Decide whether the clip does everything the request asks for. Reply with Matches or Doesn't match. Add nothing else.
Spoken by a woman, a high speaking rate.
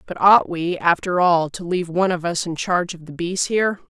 Matches